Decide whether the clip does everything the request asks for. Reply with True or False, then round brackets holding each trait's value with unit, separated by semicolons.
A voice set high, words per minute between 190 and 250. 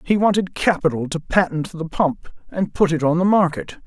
False (170 Hz; 200 wpm)